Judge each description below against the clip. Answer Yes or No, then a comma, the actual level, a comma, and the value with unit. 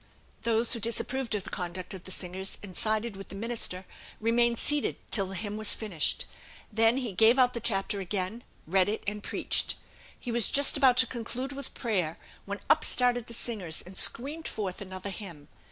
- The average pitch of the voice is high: Yes, high, 215 Hz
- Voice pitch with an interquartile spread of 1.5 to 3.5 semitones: No, average, 3.9 semitones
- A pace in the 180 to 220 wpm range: Yes, average, 190 wpm